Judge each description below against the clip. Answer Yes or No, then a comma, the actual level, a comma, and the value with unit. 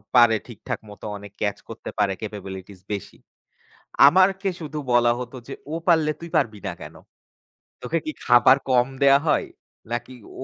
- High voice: No, low, 120 Hz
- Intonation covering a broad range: Yes, wide, 6.6 semitones